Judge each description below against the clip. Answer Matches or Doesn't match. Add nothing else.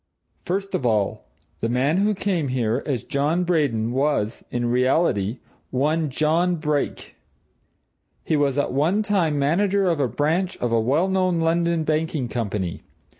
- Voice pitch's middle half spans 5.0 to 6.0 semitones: Matches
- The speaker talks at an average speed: Matches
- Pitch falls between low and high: Matches